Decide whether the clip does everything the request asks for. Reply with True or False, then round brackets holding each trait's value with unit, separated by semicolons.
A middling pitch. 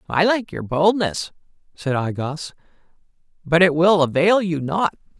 True (170 Hz)